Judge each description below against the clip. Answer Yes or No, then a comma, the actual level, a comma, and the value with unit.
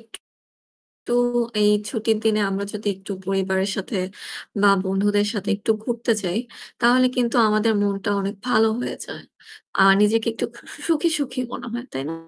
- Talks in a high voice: Yes, high, 210 Hz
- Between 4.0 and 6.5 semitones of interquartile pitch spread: No, average, 2.9 semitones